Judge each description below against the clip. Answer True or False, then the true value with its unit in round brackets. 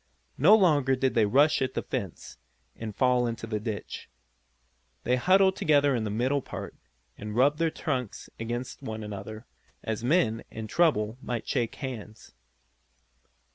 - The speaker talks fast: False (150 wpm)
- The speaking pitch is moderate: False (125 Hz)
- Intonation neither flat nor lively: True (4.4 semitones)